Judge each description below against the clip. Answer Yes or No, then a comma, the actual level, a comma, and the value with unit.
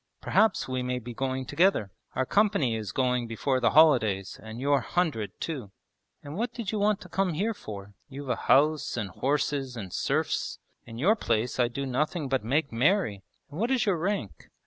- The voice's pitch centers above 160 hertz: No, low, 135 Hz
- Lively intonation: Yes, wide, 6.5 semitones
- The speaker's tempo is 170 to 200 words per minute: Yes, average, 190 wpm